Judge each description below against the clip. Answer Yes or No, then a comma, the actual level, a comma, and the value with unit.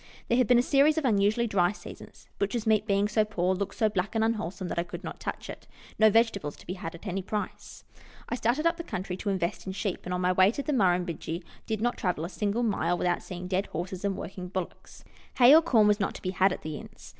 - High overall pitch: Yes, high, 200 Hz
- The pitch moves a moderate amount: Yes, average, 3.7 semitones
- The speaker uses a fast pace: Yes, fast, 255 wpm